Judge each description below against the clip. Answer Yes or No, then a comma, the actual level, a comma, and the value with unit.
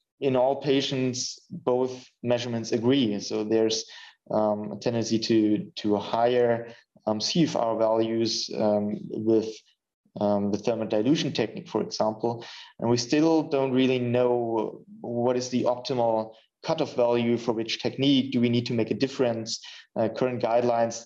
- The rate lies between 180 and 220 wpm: No, average, 150 wpm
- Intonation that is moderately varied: No, narrow, 2.2 semitones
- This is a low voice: Yes, low, 120 Hz